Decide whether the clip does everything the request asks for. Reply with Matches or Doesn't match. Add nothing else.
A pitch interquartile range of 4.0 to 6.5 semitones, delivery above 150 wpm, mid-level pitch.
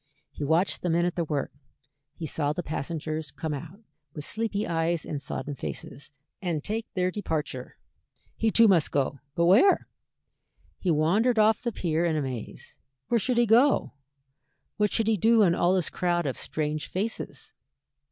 Matches